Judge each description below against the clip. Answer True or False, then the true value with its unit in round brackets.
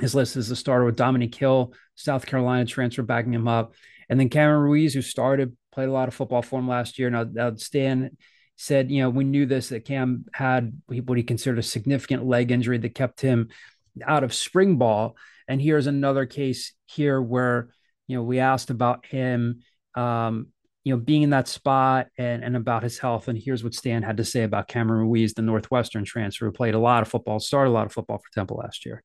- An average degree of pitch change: False (2.0 semitones)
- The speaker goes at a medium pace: False (220 wpm)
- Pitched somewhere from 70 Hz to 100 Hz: False (125 Hz)